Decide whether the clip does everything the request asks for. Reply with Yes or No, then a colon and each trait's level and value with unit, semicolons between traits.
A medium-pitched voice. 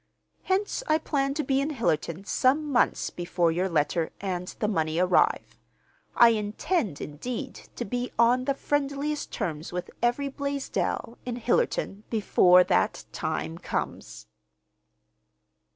No: high, 235 Hz